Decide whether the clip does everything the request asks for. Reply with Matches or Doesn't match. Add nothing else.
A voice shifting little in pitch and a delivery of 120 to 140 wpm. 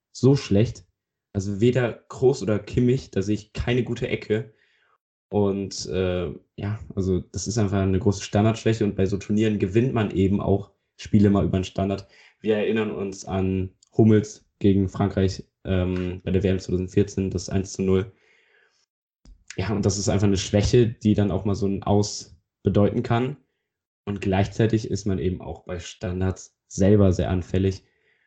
Doesn't match